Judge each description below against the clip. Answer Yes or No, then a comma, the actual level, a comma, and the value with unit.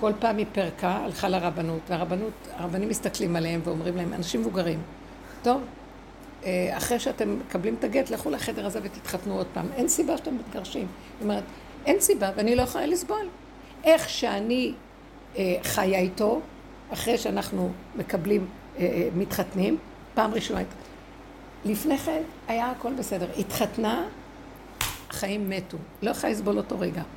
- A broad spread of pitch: Yes, wide, 5.8 semitones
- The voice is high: Yes, high, 205 Hz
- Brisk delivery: No, average, 135 wpm